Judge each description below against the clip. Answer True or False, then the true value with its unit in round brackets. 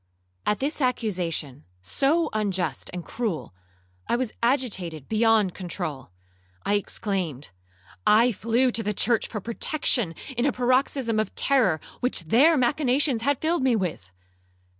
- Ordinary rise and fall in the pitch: False (5.8 semitones)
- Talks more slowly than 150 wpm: True (135 wpm)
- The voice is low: False (225 Hz)